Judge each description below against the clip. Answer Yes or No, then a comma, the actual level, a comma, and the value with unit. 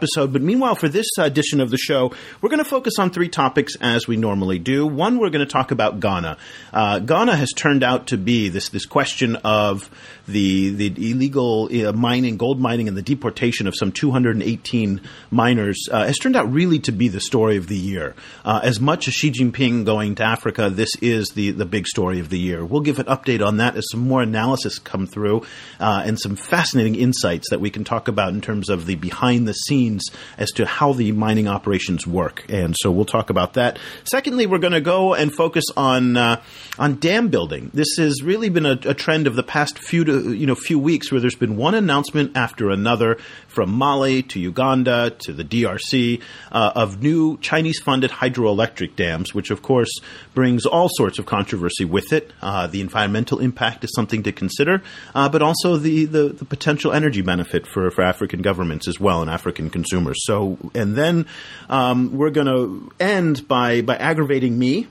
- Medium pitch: No, low, 120 Hz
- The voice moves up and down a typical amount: No, wide, 5.8 semitones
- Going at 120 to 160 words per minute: No, average, 200 wpm